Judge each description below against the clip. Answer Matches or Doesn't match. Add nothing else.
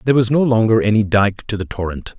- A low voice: Matches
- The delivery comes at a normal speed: Doesn't match